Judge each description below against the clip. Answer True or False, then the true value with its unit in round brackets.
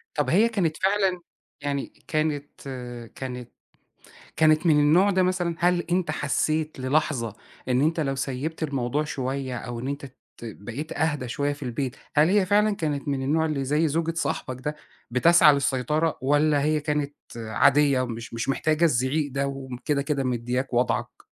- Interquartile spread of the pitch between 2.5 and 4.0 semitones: True (3.3 semitones)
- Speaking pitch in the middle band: True (145 Hz)